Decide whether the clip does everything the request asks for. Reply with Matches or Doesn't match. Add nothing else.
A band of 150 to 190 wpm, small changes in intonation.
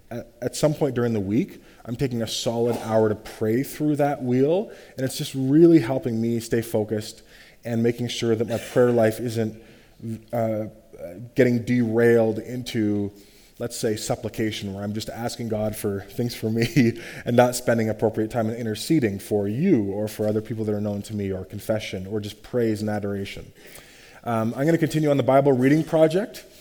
Matches